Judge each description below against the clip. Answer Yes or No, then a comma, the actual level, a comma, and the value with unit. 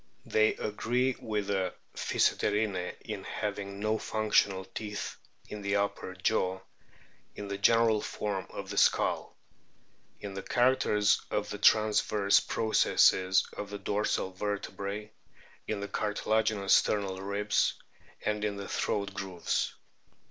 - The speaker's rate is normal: No, slow, 125 wpm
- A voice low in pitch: Yes, low, 105 Hz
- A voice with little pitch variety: Yes, narrow, 1.4 semitones